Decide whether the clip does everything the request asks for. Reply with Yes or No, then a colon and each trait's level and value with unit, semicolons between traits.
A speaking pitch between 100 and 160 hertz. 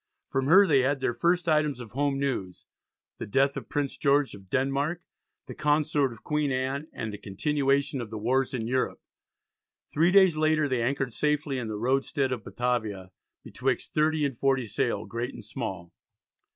Yes: low, 135 Hz